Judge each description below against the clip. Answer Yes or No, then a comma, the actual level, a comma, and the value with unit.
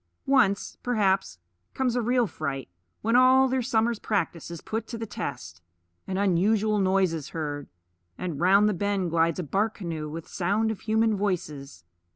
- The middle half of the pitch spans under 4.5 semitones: No, average, 5.2 semitones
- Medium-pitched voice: No, high, 195 Hz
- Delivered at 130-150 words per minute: No, average, 170 wpm